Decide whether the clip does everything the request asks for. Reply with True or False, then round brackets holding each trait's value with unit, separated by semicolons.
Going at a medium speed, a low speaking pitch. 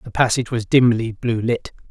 True (190 wpm; 115 Hz)